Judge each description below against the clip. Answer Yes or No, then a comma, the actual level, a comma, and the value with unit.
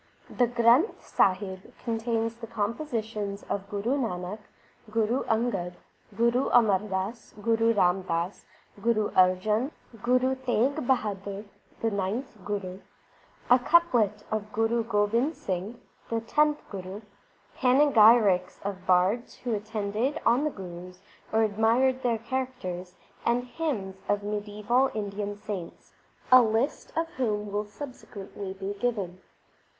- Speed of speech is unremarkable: No, slow, 125 wpm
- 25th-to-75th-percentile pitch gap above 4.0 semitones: No, average, 3.5 semitones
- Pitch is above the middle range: Yes, high, 215 Hz